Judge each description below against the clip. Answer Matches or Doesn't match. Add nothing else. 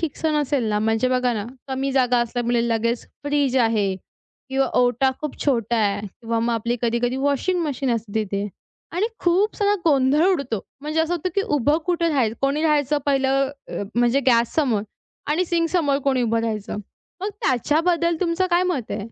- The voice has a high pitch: Matches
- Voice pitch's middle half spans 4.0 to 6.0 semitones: Matches